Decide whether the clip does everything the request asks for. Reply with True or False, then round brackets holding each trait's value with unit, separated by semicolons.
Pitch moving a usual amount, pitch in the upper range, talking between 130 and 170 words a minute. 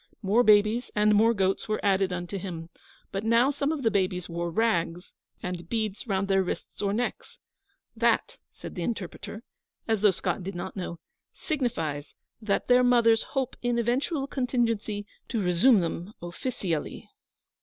True (4.6 semitones; 210 Hz; 155 wpm)